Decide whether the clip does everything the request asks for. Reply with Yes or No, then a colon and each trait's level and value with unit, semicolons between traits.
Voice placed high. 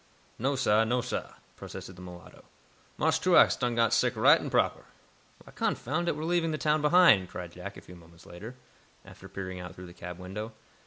No: low, 110 Hz